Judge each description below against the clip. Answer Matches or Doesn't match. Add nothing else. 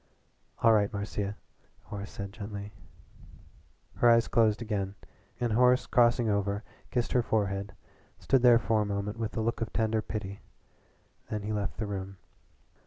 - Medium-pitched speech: Doesn't match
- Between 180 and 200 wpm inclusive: Doesn't match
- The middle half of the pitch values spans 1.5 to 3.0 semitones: Matches